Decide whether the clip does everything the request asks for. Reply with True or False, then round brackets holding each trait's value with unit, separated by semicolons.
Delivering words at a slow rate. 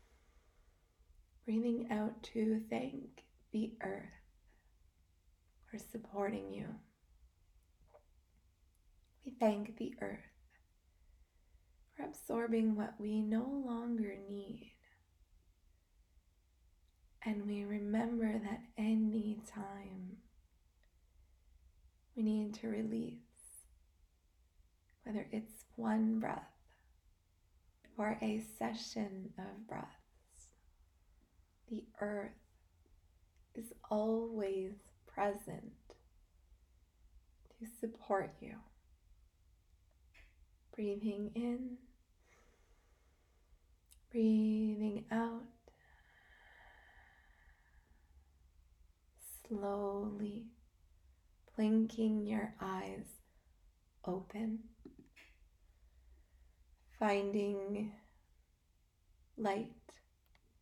True (55 wpm)